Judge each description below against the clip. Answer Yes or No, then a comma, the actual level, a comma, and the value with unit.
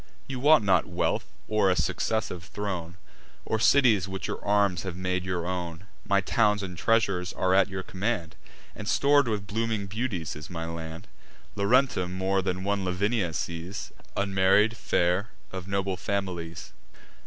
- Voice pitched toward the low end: Yes, very low, 95 Hz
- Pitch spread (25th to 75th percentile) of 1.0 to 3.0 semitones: Yes, narrow, 2.6 semitones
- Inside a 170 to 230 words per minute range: No, average, 155 wpm